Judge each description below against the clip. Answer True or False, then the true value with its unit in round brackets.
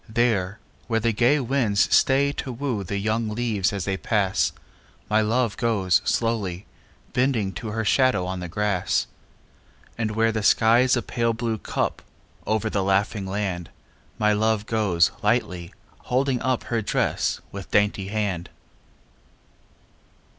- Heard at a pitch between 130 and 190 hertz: False (110 Hz)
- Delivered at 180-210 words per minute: False (140 wpm)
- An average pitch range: True (3.0 semitones)